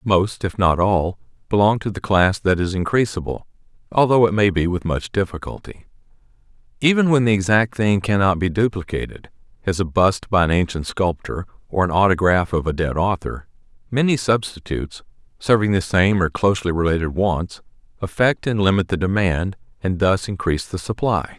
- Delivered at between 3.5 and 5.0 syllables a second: No, 5.3 syllables/s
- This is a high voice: No, very low, 95 Hz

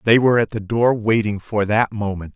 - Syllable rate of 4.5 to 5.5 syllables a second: Yes, 5.4 syllables/s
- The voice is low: Yes, low, 110 Hz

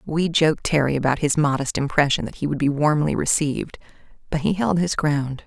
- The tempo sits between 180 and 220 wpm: Yes, average, 200 wpm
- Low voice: No, medium, 150 Hz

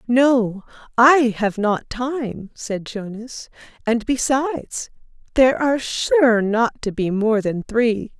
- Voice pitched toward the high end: Yes, high, 235 Hz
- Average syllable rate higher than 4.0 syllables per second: No, 3.4 syllables/s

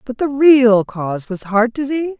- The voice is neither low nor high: No, high, 245 Hz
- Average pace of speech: Yes, average, 190 wpm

